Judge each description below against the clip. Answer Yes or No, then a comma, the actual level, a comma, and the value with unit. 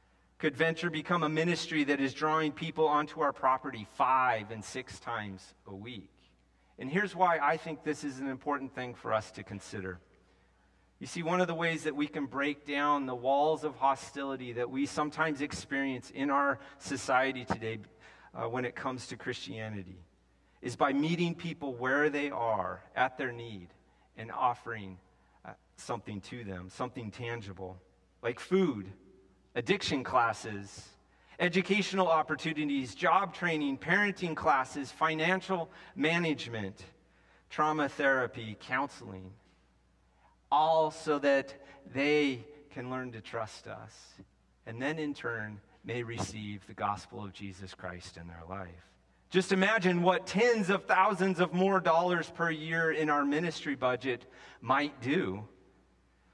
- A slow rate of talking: No, average, 145 wpm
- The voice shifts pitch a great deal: Yes, wide, 8.2 semitones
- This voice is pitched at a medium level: No, low, 125 Hz